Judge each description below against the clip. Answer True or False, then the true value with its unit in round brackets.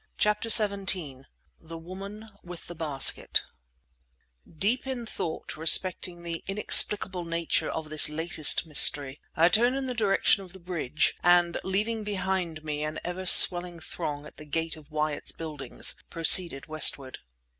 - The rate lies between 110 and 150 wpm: True (145 wpm)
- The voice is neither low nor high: True (170 Hz)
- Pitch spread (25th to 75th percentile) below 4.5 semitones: True (4.0 semitones)